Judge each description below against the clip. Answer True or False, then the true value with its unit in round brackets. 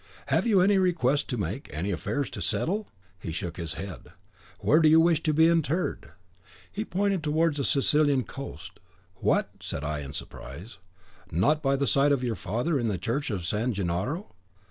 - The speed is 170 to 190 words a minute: True (185 wpm)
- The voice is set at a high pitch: False (140 Hz)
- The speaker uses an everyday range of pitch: False (8.5 semitones)